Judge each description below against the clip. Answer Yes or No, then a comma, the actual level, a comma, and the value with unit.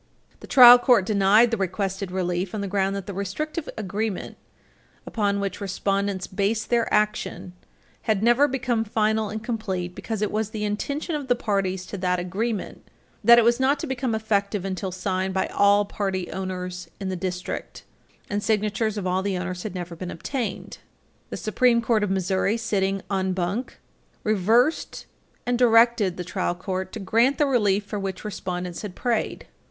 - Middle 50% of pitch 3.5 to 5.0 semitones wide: No, average, 3.1 semitones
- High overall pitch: Yes, high, 200 Hz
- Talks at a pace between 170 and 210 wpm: Yes, average, 175 wpm